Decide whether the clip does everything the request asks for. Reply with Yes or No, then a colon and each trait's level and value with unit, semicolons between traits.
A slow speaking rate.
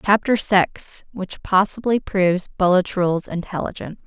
Yes: slow, 90 wpm